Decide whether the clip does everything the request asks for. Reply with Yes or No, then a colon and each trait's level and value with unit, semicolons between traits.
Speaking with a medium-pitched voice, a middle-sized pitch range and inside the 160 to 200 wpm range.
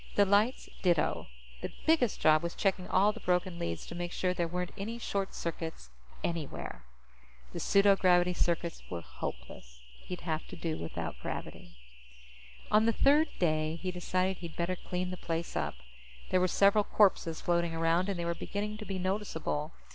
Yes: medium, 180 Hz; average, 3.1 semitones; average, 170 wpm